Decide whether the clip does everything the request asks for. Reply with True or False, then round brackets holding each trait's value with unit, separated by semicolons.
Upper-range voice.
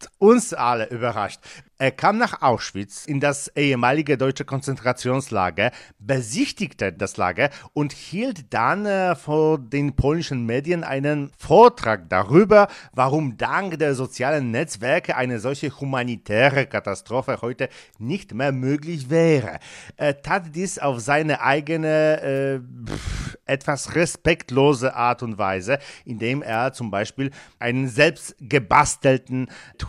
False (135 Hz)